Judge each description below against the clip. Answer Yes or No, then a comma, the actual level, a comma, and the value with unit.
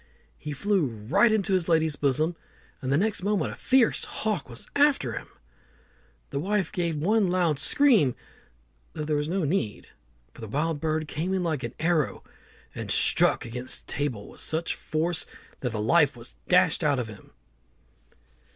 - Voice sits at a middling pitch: Yes, medium, 160 Hz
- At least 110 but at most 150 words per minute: No, average, 170 wpm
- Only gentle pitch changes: No, wide, 5.5 semitones